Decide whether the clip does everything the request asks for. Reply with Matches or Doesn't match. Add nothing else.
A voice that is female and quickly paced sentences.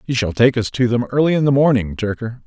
Doesn't match